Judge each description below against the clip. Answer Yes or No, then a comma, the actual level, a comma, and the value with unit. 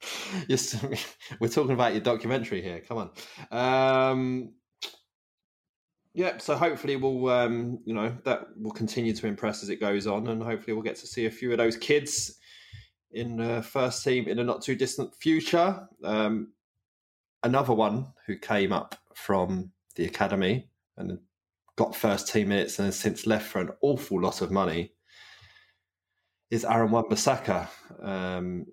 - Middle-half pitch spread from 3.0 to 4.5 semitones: Yes, average, 3.5 semitones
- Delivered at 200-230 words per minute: No, average, 160 wpm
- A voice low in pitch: Yes, low, 115 Hz